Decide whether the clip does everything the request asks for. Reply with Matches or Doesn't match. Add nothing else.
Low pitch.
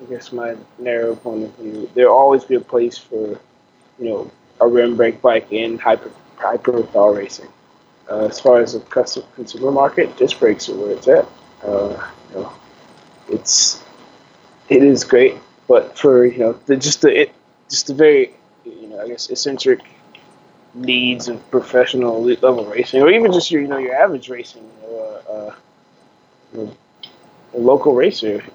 Matches